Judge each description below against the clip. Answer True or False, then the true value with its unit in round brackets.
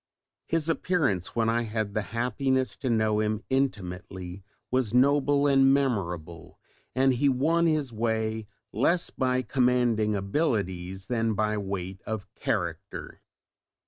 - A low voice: True (115 Hz)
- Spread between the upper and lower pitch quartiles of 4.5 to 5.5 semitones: True (4.8 semitones)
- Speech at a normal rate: False (125 wpm)